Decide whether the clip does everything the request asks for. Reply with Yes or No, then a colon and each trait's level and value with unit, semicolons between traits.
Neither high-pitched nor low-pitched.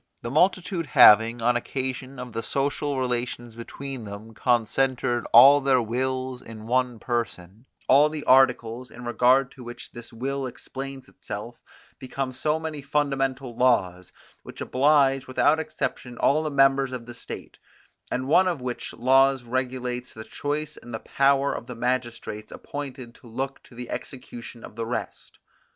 No: low, 130 Hz